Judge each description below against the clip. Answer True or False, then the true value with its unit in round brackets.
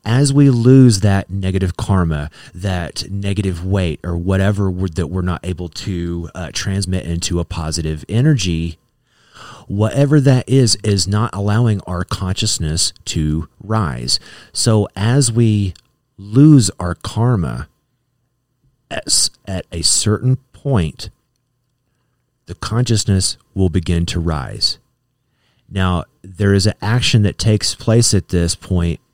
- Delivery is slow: True (125 wpm)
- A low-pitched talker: True (100 Hz)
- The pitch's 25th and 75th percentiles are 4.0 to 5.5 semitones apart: True (5.1 semitones)